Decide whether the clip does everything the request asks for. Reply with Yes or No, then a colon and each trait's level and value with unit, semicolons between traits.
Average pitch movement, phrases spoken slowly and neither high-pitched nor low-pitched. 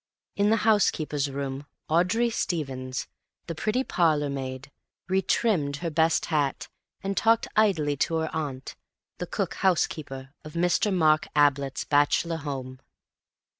Yes: average, 4.5 semitones; slow, 130 wpm; medium, 155 Hz